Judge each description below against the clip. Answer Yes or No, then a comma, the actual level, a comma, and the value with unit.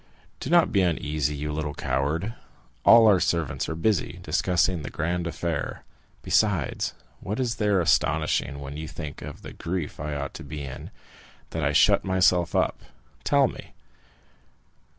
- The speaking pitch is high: No, very low, 80 Hz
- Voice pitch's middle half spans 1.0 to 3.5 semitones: No, average, 4.0 semitones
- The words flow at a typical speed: Yes, average, 150 wpm